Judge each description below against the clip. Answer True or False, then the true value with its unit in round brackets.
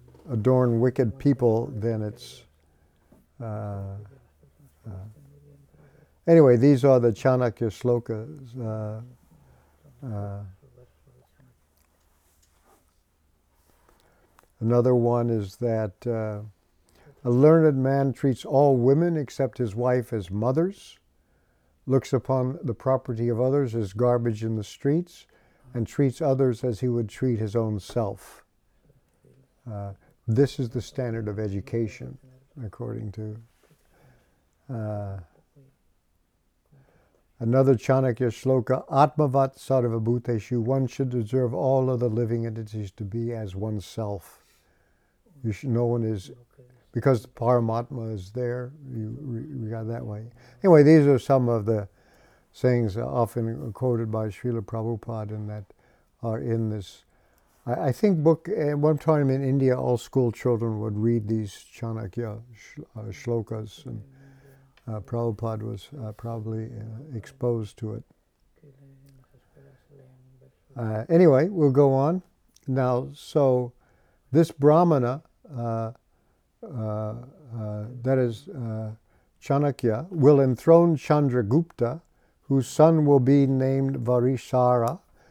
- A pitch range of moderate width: True (3.5 semitones)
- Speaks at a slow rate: True (115 wpm)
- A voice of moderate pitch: False (120 Hz)